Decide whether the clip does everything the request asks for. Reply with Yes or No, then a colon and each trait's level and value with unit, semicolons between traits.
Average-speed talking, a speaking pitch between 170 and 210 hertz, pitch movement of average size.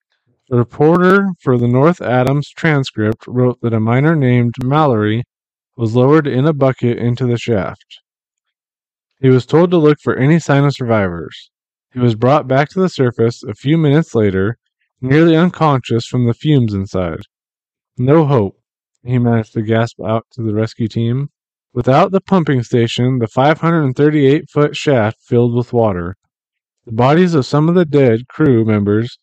No: average, 160 wpm; low, 125 Hz; average, 4.4 semitones